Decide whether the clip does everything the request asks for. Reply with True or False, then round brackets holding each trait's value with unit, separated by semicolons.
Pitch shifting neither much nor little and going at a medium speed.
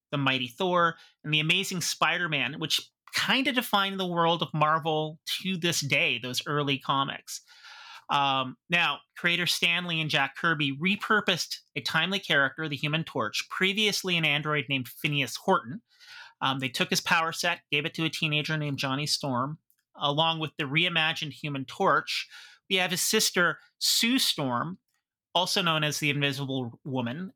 True (4.0 semitones; 160 wpm)